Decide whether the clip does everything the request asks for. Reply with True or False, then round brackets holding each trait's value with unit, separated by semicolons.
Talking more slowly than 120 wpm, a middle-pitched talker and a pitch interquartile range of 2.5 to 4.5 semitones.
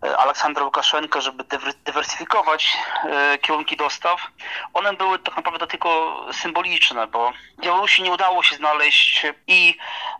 True (110 wpm; 165 Hz; 3.7 semitones)